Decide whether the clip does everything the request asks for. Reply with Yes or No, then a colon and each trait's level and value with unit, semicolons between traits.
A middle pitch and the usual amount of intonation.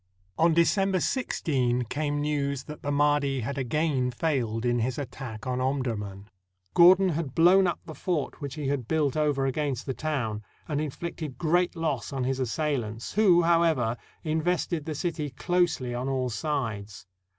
Yes: medium, 145 Hz; average, 4.2 semitones